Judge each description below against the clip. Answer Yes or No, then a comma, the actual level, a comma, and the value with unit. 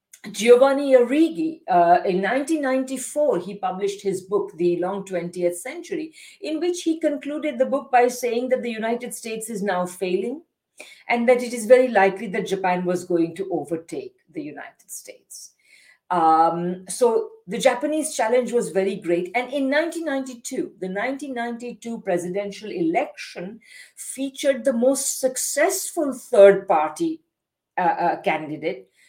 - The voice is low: No, high, 245 Hz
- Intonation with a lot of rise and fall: Yes, wide, 7.2 semitones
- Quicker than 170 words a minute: No, average, 140 wpm